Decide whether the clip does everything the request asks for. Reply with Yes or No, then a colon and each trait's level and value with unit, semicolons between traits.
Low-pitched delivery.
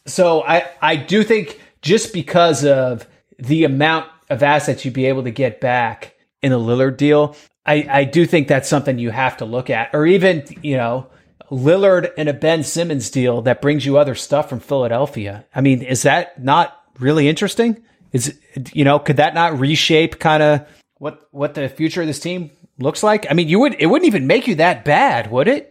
No: medium, 150 Hz